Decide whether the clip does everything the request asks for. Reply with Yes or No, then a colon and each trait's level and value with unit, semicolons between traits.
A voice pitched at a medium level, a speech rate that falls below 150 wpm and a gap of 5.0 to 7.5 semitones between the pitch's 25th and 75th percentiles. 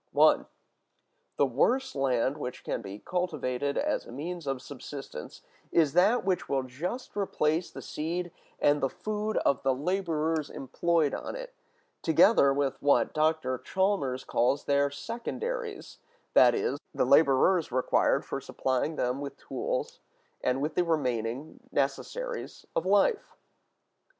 Yes: medium, 150 Hz; slow, 135 wpm; average, 5.3 semitones